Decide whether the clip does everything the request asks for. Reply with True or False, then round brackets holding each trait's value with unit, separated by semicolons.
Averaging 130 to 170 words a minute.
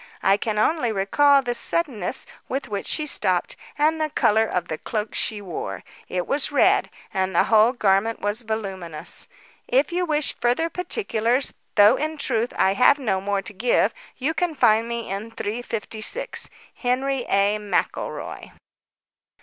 True (155 wpm)